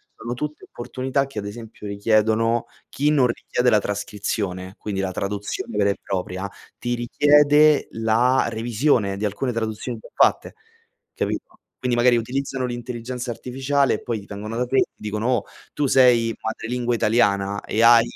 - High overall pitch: No, low, 115 Hz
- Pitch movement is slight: No, average, 3.3 semitones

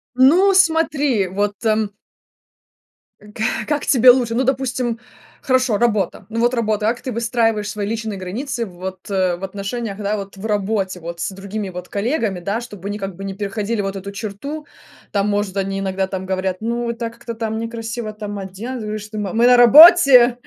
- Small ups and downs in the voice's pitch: No, average, 3.3 semitones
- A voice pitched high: Yes, high, 215 Hz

